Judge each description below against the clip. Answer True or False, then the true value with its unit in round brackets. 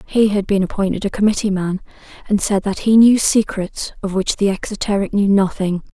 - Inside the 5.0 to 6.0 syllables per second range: True (5.4 syllables/s)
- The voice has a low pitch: False (200 Hz)